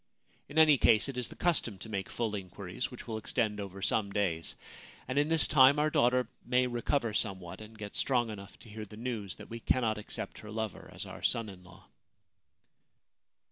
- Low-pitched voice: Yes, low, 110 Hz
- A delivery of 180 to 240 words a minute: Yes, average, 200 wpm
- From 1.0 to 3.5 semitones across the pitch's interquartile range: No, average, 3.9 semitones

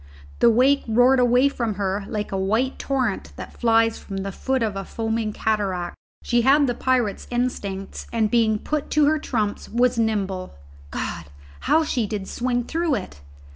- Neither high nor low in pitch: No, high, 230 Hz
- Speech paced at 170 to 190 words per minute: Yes, average, 175 wpm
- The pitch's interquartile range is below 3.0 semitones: No, average, 3.7 semitones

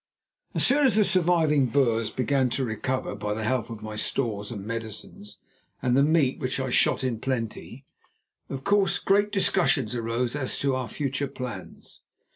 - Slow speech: No, average, 170 wpm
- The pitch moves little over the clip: No, average, 4.1 semitones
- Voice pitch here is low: Yes, low, 130 Hz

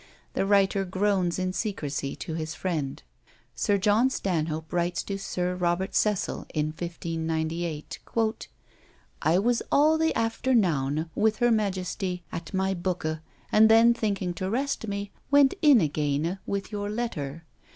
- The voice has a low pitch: No, medium, 185 Hz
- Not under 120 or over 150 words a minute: Yes, average, 140 wpm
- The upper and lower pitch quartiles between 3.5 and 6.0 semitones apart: Yes, average, 4.4 semitones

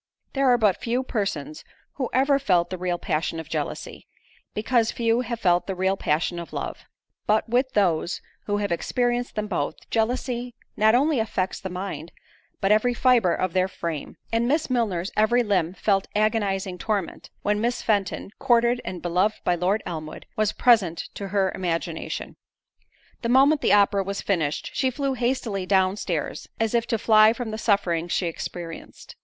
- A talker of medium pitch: No, high, 205 Hz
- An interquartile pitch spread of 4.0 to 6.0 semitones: Yes, average, 4.7 semitones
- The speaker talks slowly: No, average, 170 wpm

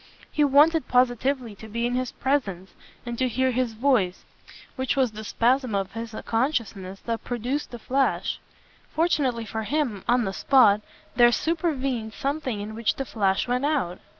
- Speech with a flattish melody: No, average, 3.7 semitones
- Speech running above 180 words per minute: No, average, 165 wpm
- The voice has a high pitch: Yes, high, 245 Hz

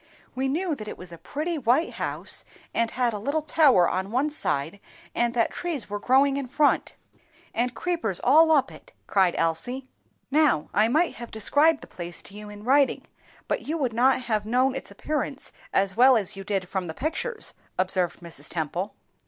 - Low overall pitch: No, high, 240 Hz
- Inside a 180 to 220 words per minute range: Yes, average, 190 wpm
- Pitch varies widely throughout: Yes, wide, 6.6 semitones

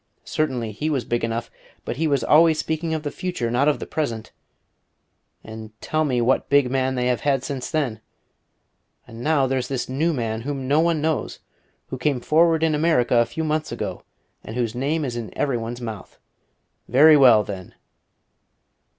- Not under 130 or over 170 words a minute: No, average, 185 wpm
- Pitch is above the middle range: No, low, 135 Hz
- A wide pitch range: No, average, 4.6 semitones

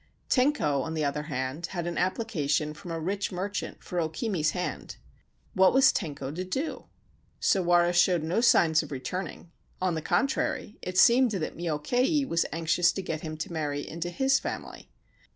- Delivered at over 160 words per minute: Yes, average, 170 wpm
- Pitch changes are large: No, average, 3.8 semitones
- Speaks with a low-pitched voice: No, medium, 175 Hz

